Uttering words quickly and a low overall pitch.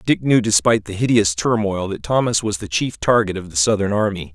Yes: fast, 220 wpm; low, 105 Hz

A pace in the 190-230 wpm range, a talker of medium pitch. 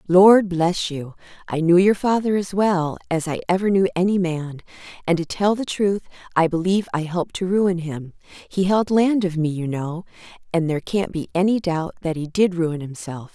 Yes: average, 200 wpm; medium, 175 Hz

